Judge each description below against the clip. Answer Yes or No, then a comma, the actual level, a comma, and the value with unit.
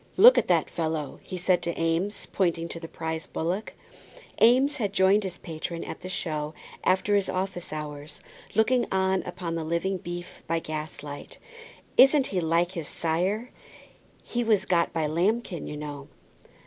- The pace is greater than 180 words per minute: No, average, 160 wpm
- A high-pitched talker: No, medium, 175 Hz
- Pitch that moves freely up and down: No, average, 3.3 semitones